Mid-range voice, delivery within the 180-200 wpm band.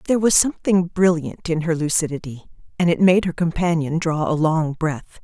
Yes: medium, 165 Hz; average, 185 wpm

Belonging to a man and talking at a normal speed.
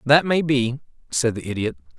Yes: male; average, 180 wpm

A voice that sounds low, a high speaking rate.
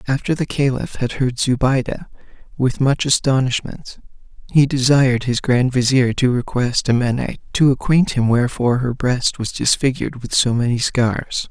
No: low, 130 Hz; average, 150 wpm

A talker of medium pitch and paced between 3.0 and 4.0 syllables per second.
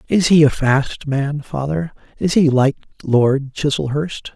Yes: medium, 145 Hz; 3.9 syllables/s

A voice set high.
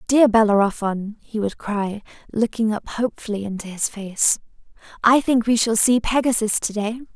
Yes: high, 220 Hz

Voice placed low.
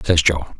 Yes: very low, 80 Hz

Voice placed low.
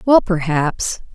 No: medium, 185 Hz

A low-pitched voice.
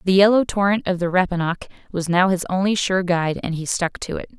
No: medium, 185 Hz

